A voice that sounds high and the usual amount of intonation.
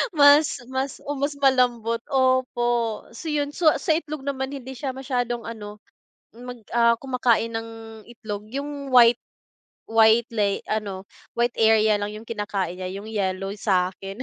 Yes: high, 235 Hz; average, 3.8 semitones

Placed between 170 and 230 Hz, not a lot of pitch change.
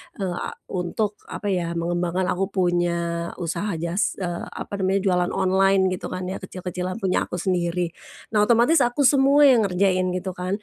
Yes: medium, 185 Hz; narrow, 2.2 semitones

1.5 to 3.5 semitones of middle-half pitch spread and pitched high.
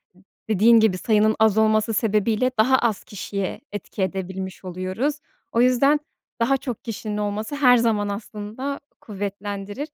Yes: average, 2.8 semitones; high, 215 Hz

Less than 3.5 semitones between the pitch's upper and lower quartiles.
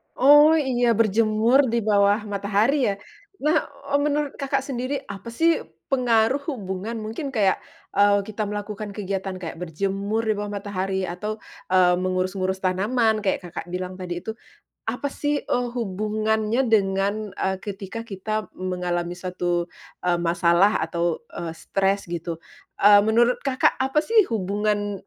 No: average, 3.8 semitones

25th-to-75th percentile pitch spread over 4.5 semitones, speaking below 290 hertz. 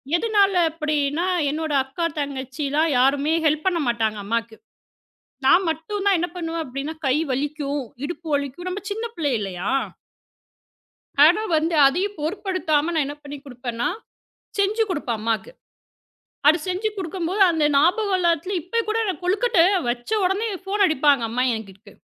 No: average, 5.1 semitones; very high, 315 Hz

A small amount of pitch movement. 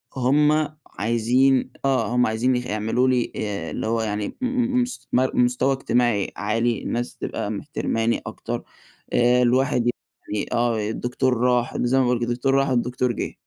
Yes: narrow, 2.3 semitones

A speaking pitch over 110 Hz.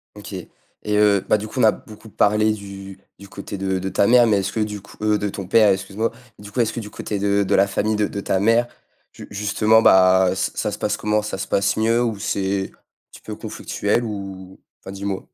No: low, 100 Hz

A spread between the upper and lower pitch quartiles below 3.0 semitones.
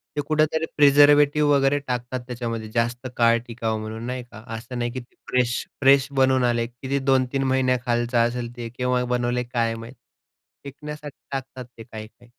Yes: narrow, 2.4 semitones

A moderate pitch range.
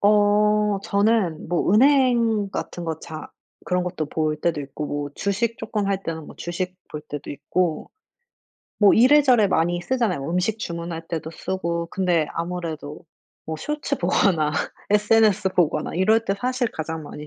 Yes: average, 4.6 semitones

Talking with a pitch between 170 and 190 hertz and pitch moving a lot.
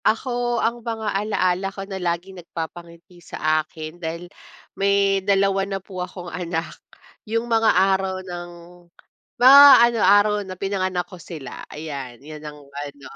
No: medium, 185 Hz; average, 3.1 semitones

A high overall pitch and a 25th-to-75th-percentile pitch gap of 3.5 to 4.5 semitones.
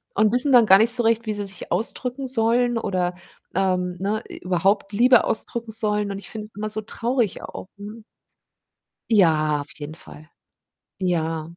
Yes: high, 210 Hz; average, 4.0 semitones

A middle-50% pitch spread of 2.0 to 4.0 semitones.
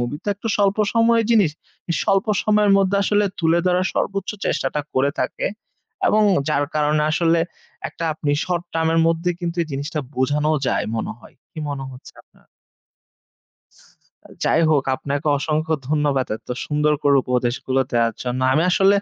No: average, 4.6 semitones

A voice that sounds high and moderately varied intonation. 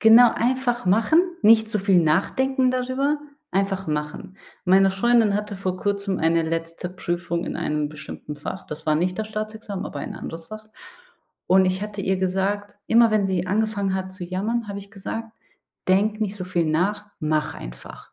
Yes: high, 195 Hz; average, 3.3 semitones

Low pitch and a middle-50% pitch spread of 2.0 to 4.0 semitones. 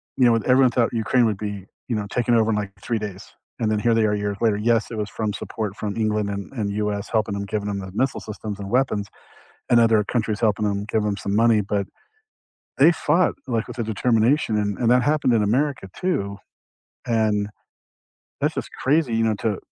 Yes: low, 110 Hz; narrow, 2.5 semitones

